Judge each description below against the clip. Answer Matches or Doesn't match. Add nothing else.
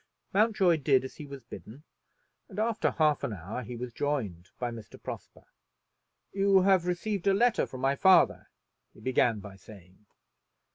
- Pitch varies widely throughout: Matches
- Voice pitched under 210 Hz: Matches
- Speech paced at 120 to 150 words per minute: Doesn't match